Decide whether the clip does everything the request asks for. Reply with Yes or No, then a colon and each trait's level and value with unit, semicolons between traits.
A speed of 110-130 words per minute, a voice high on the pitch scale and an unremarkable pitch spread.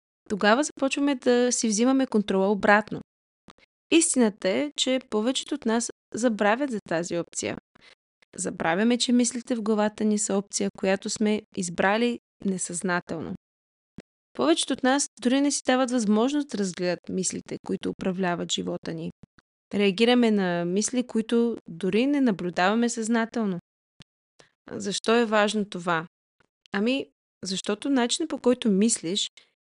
Yes: average, 125 wpm; high, 220 Hz; average, 4.1 semitones